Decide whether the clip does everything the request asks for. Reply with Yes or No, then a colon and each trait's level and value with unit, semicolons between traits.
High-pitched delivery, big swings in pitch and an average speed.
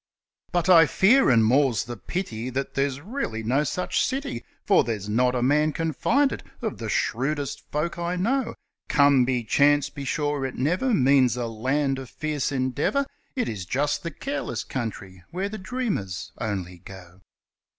No: medium, 140 Hz; wide, 6.3 semitones; average, 170 wpm